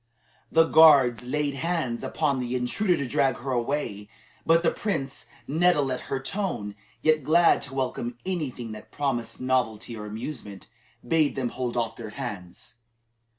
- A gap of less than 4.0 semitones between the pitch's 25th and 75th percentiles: No, average, 4.4 semitones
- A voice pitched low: Yes, low, 130 Hz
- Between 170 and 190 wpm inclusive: No, average, 155 wpm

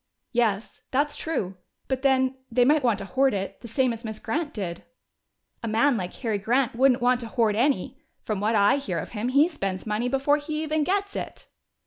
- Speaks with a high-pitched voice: Yes, high, 245 Hz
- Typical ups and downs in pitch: Yes, average, 4.6 semitones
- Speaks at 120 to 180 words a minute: No, fast, 205 wpm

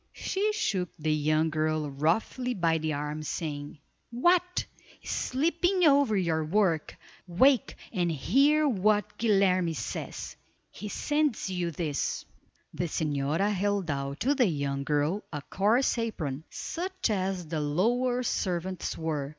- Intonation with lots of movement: Yes, wide, 7.8 semitones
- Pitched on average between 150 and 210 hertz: Yes, medium, 185 Hz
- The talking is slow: Yes, slow, 130 wpm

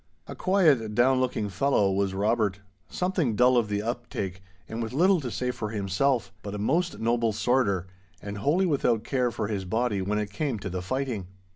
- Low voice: Yes, low, 115 Hz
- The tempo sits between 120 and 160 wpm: No, average, 190 wpm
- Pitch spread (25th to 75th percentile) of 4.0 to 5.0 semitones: Yes, average, 4.4 semitones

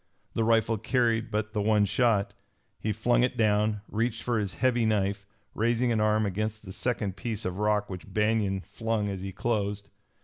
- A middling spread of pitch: No, narrow, 2.0 semitones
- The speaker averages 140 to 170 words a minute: No, average, 180 wpm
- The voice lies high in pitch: No, low, 110 Hz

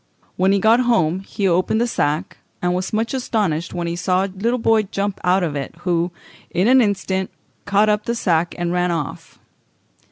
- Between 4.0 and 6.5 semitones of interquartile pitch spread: No, average, 3.6 semitones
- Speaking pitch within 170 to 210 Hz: Yes, high, 190 Hz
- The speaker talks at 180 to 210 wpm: Yes, average, 195 wpm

